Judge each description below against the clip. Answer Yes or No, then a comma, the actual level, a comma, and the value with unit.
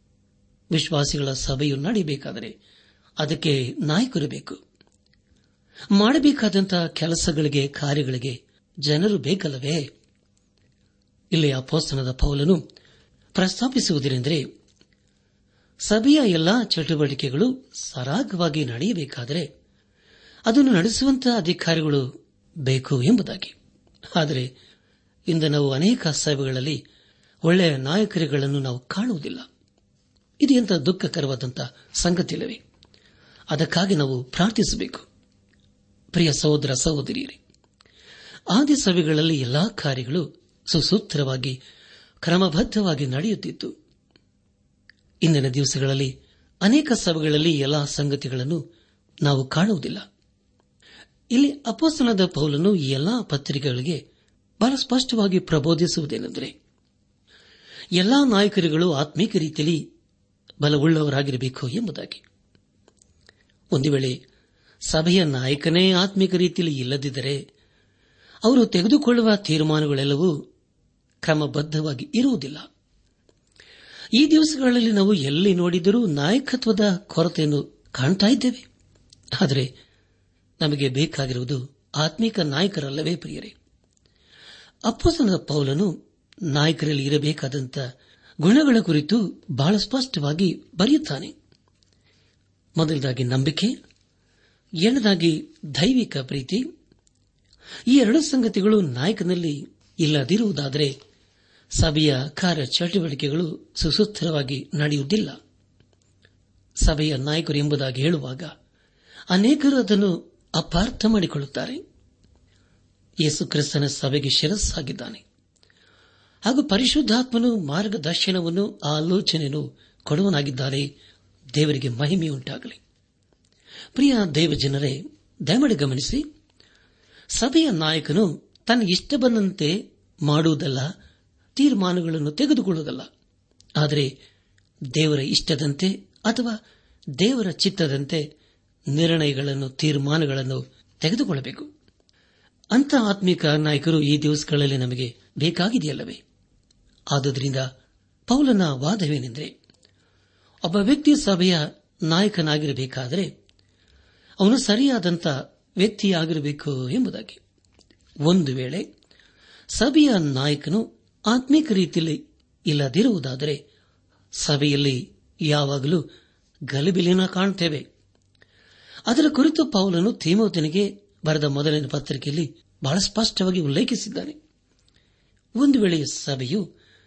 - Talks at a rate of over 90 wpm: No, average, 70 wpm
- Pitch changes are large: Yes, wide, 6.2 semitones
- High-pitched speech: No, medium, 155 Hz